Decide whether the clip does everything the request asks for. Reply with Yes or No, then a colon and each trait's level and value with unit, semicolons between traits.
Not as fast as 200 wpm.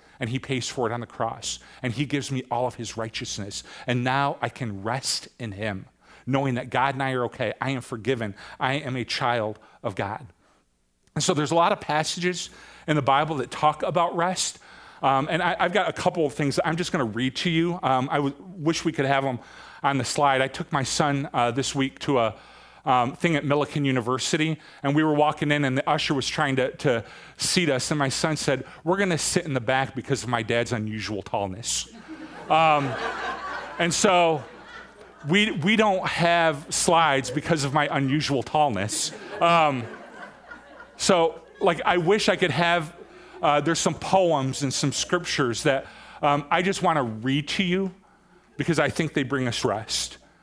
No: fast, 205 wpm